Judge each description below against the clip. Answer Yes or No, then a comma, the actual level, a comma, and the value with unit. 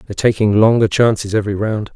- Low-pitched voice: Yes, low, 105 Hz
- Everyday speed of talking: Yes, average, 185 wpm